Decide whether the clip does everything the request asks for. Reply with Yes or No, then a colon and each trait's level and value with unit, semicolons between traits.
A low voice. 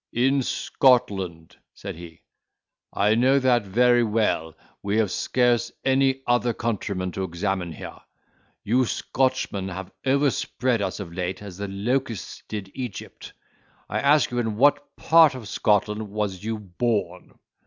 Yes: low, 110 Hz